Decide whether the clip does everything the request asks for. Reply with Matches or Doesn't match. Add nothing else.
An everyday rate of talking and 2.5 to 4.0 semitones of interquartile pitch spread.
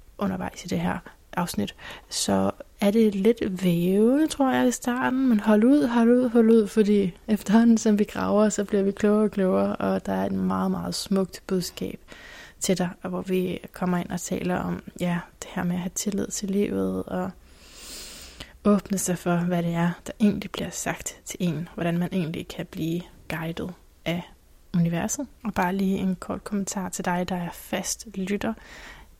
Matches